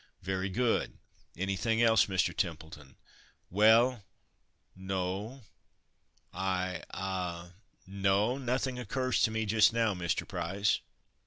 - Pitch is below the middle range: Yes, low, 100 Hz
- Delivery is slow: Yes, slow, 100 wpm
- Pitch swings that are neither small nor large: Yes, average, 3.5 semitones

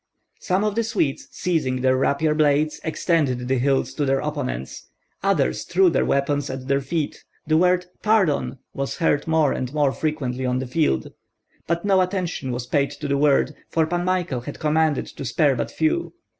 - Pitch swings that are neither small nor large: Yes, average, 4.1 semitones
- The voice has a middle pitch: Yes, medium, 145 Hz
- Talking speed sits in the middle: Yes, average, 185 wpm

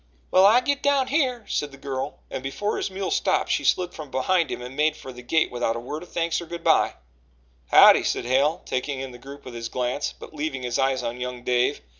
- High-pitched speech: No, medium, 140 Hz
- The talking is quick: Yes, fast, 240 wpm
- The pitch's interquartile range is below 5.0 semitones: No, wide, 5.5 semitones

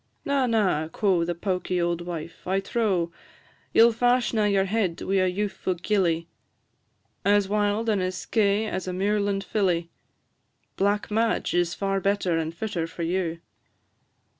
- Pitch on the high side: Yes, high, 195 Hz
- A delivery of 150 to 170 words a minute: Yes, average, 155 wpm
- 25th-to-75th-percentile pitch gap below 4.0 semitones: Yes, average, 3.2 semitones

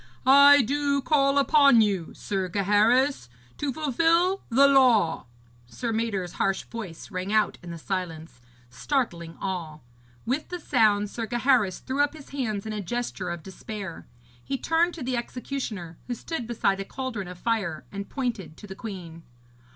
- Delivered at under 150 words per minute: No, average, 160 wpm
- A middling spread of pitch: No, wide, 6.3 semitones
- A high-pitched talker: Yes, high, 225 Hz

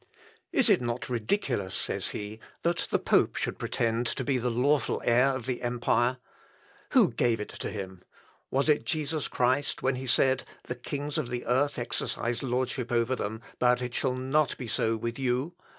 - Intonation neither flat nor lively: No, narrow, 2.3 semitones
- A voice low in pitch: Yes, low, 125 Hz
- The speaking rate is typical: Yes, average, 180 wpm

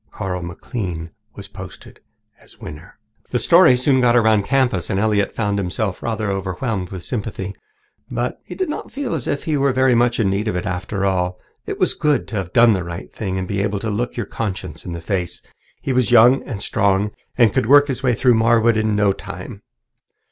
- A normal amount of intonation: Yes, average, 4.3 semitones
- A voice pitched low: Yes, low, 110 Hz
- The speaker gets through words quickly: Yes, fast, 215 wpm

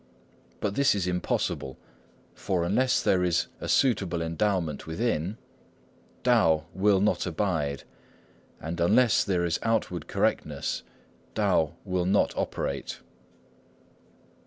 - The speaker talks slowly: Yes, slow, 110 wpm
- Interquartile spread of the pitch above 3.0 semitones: Yes, average, 3.8 semitones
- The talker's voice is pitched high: No, very low, 90 Hz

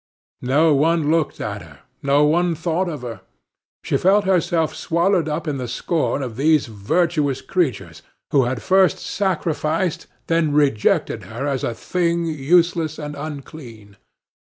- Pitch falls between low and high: Yes, medium, 155 Hz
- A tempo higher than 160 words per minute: No, average, 145 wpm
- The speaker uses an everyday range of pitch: Yes, average, 3.9 semitones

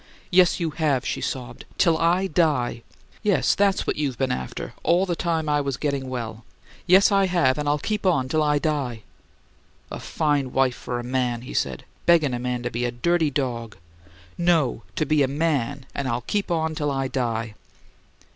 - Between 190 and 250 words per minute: Yes, average, 195 wpm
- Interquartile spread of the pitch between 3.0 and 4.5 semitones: No, average, 5.0 semitones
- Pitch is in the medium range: Yes, medium, 145 Hz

